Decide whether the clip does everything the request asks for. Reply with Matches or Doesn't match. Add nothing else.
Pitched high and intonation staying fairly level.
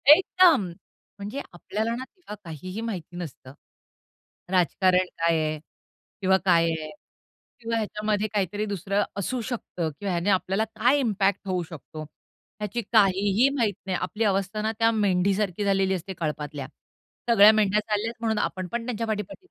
Doesn't match